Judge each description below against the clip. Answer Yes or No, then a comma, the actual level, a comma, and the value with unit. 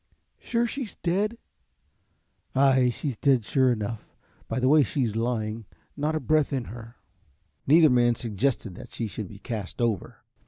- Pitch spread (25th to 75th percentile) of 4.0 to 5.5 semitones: Yes, average, 4.6 semitones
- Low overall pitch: Yes, low, 125 Hz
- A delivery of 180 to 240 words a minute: No, average, 155 wpm